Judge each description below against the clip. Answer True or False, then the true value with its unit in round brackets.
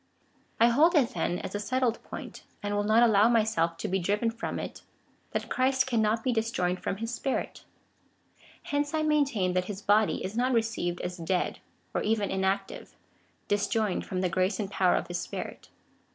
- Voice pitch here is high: True (215 Hz)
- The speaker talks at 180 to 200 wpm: True (185 wpm)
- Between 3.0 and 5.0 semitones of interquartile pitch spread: True (3.9 semitones)